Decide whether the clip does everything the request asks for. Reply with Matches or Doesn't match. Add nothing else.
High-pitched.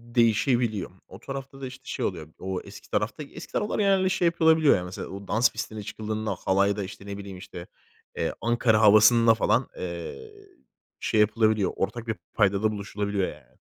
Doesn't match